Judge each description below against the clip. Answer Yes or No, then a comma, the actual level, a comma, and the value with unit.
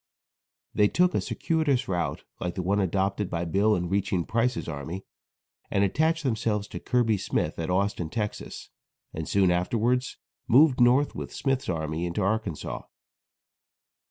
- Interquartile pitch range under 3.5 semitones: No, wide, 5.6 semitones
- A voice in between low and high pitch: No, low, 100 Hz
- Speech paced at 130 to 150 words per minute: Yes, average, 145 wpm